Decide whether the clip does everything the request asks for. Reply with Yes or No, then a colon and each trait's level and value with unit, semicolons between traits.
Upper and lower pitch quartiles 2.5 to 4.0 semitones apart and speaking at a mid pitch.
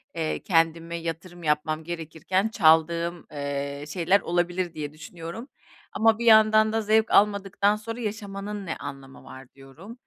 No: average, 4.9 semitones; medium, 170 Hz